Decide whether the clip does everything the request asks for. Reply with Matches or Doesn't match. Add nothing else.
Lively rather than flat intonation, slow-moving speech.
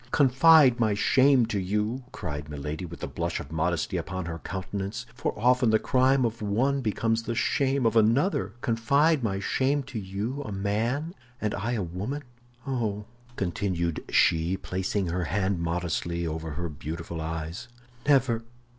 Doesn't match